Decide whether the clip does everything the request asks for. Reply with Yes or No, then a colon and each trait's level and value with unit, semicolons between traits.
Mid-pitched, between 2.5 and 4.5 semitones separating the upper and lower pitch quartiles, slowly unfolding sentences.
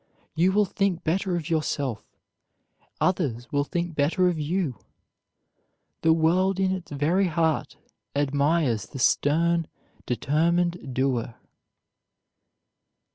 Yes: medium, 160 Hz; average, 3.7 semitones; slow, 105 wpm